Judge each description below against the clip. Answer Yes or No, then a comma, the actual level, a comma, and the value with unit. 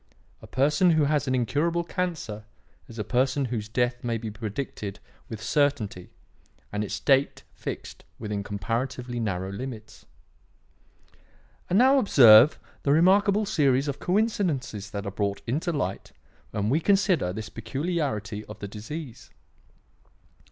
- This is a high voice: No, low, 125 Hz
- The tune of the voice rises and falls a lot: Yes, wide, 6.4 semitones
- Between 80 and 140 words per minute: Yes, slow, 135 wpm